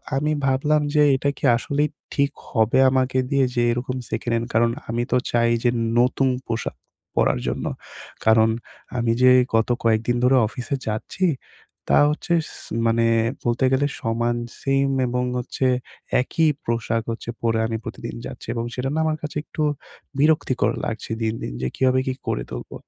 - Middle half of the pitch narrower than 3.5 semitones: Yes, average, 2.9 semitones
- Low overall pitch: Yes, low, 120 Hz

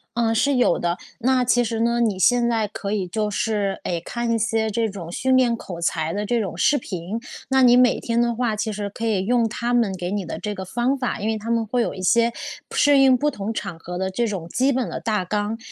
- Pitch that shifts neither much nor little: Yes, average, 3.3 semitones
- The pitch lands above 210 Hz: Yes, high, 225 Hz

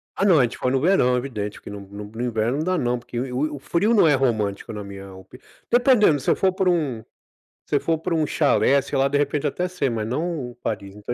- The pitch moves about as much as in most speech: No, wide, 6.2 semitones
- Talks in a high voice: No, low, 135 Hz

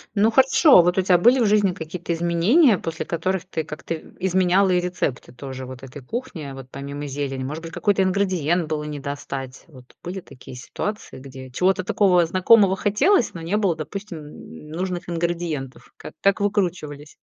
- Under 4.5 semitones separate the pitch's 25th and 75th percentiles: No, average, 4.9 semitones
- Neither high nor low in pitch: Yes, medium, 170 Hz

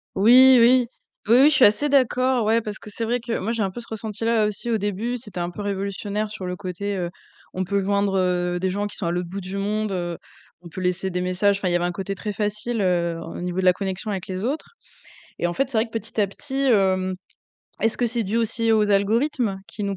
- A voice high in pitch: Yes, high, 205 Hz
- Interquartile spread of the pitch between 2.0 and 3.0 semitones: No, average, 3.5 semitones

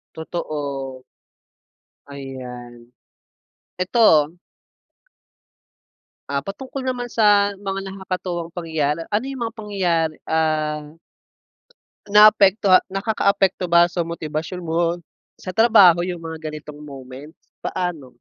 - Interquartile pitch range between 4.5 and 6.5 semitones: Yes, average, 4.8 semitones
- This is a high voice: No, medium, 170 Hz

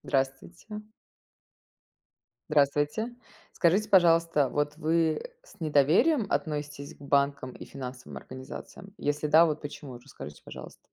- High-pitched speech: No, medium, 150 Hz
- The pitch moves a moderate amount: Yes, average, 3.1 semitones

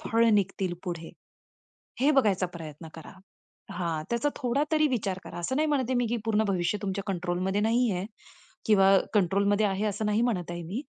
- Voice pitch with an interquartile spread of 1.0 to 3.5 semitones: No, average, 4.6 semitones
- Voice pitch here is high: Yes, high, 200 Hz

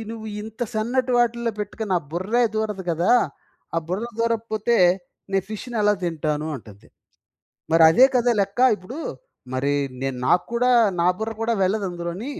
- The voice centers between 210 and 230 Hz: Yes, high, 215 Hz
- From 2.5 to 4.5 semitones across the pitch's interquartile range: No, average, 5.2 semitones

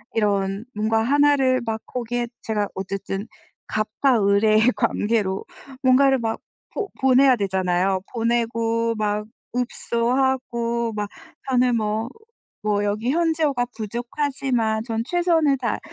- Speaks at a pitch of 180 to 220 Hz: No, high, 230 Hz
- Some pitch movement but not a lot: Yes, average, 3.3 semitones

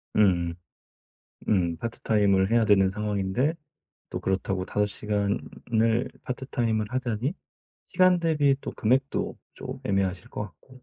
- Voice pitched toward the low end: Yes, low, 105 Hz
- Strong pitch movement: No, average, 4.5 semitones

